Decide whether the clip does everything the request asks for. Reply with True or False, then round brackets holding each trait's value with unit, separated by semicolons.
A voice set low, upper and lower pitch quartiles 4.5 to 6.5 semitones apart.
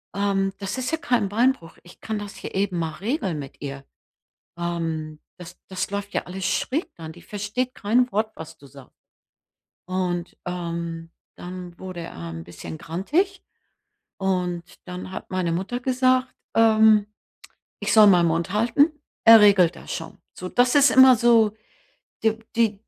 False (195 Hz; 4.8 semitones)